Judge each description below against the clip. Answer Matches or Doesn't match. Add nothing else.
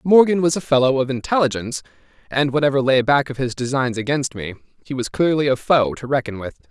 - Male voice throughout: Matches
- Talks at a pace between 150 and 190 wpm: Doesn't match